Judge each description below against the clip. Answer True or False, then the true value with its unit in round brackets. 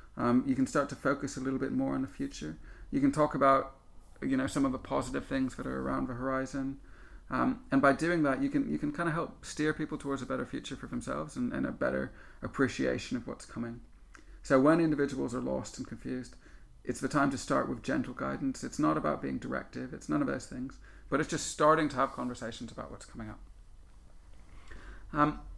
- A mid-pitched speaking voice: False (130 Hz)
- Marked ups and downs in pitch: True (7.7 semitones)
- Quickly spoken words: True (220 wpm)